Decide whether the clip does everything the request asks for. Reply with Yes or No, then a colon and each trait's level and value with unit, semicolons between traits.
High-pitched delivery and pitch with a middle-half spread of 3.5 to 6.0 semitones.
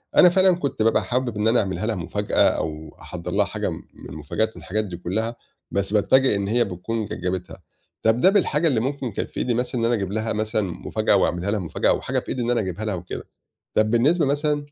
No: low, 110 Hz; average, 4.3 semitones